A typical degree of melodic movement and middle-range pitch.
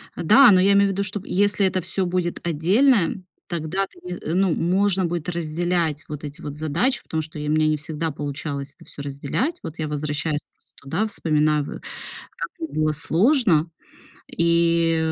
Yes: average, 3.8 semitones; medium, 165 Hz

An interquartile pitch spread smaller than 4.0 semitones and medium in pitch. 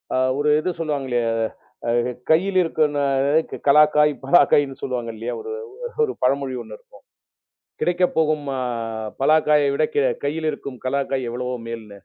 Yes: average, 3.2 semitones; medium, 145 Hz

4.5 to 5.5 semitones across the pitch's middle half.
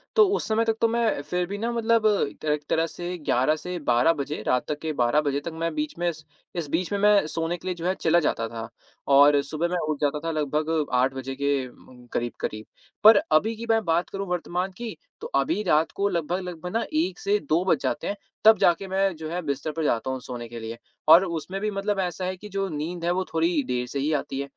Yes: average, 4.9 semitones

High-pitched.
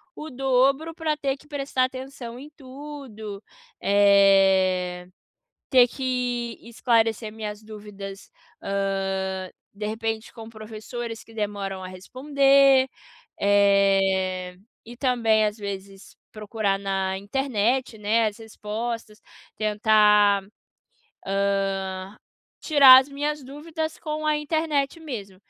Yes: high, 220 Hz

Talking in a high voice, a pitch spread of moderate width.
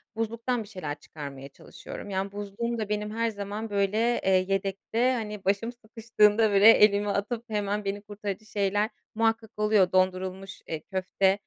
No: high, 205 Hz; narrow, 2.2 semitones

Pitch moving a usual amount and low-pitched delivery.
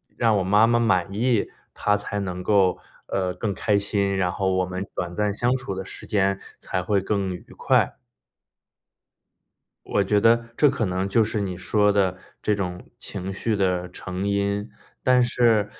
No: narrow, 2.3 semitones; low, 100 Hz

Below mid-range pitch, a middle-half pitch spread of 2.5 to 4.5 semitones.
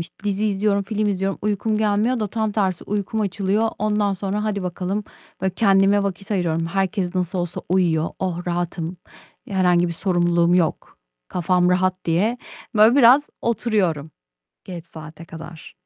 No: high, 190 Hz; average, 3.1 semitones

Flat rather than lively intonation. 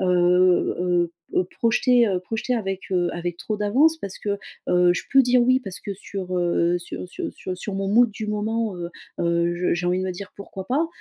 No: average, 3.6 semitones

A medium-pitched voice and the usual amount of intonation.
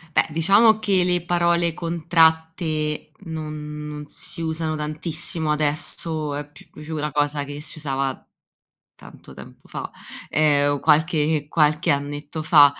No: medium, 155 Hz; narrow, 1.8 semitones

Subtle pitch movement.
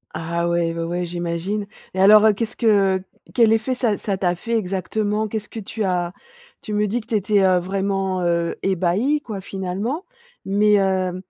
No: average, 3.1 semitones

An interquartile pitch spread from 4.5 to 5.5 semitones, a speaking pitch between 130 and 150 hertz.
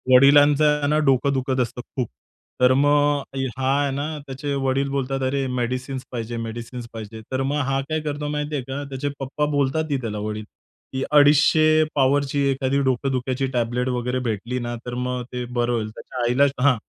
No: narrow, 2.5 semitones; low, 135 Hz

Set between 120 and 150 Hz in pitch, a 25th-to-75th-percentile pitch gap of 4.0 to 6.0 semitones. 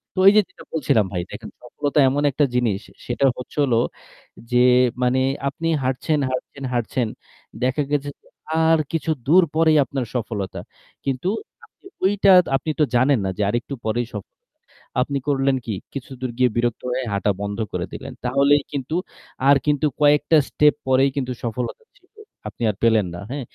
No: low, 135 Hz; average, 3.4 semitones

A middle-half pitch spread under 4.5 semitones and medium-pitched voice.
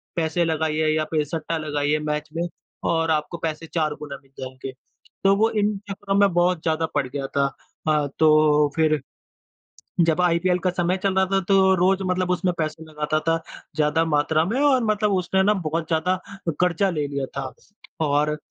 Yes: average, 3.3 semitones; medium, 160 Hz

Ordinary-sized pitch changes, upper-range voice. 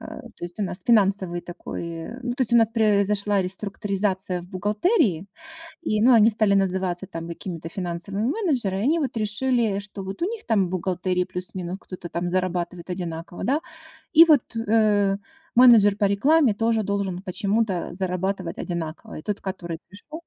Yes: average, 3.5 semitones; high, 200 Hz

